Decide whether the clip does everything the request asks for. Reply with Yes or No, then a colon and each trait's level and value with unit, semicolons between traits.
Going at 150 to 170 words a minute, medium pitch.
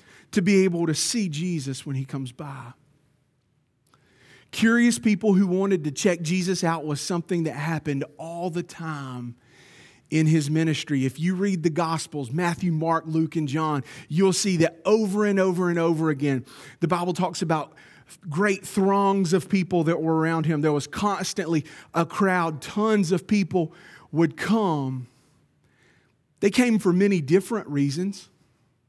Yes: average, 155 wpm; medium, 165 Hz